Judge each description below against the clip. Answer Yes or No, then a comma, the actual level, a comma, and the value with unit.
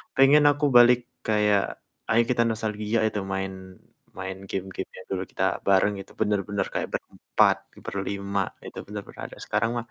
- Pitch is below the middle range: Yes, low, 105 Hz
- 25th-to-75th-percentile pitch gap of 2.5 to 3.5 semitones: Yes, average, 2.9 semitones